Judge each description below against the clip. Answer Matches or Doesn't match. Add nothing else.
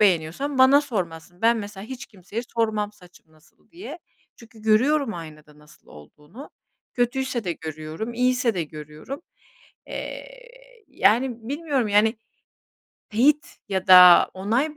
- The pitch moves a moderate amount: Doesn't match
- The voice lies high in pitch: Matches